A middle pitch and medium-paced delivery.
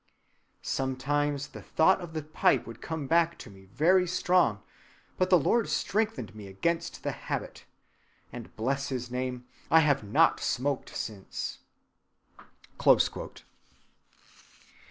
No: medium, 145 Hz; slow, 120 wpm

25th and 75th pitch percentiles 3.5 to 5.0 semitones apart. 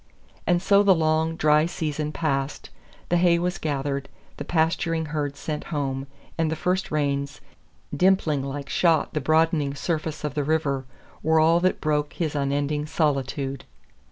No: narrow, 2.5 semitones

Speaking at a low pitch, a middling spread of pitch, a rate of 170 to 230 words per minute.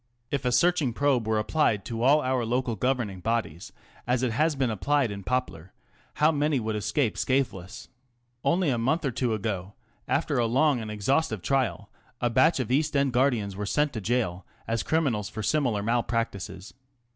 Yes: low, 120 Hz; average, 4.4 semitones; average, 180 wpm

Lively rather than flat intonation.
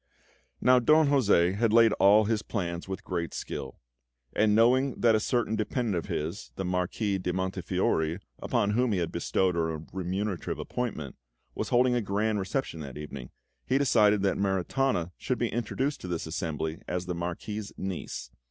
No: average, 4.8 semitones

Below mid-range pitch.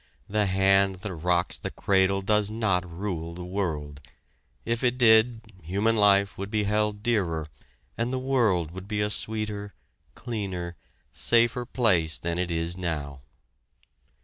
Yes: low, 100 Hz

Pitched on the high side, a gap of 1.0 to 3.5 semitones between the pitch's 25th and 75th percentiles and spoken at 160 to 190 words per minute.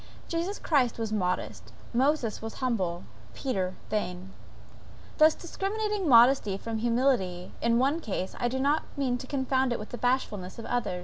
No: high, 245 Hz; average, 4.8 semitones; average, 165 wpm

